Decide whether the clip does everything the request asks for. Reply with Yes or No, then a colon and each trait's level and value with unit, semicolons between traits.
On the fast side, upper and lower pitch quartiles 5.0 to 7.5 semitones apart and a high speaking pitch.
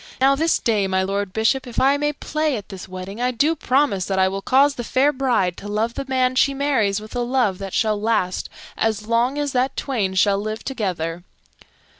Yes: fast, 215 wpm; average, 5.3 semitones; high, 230 Hz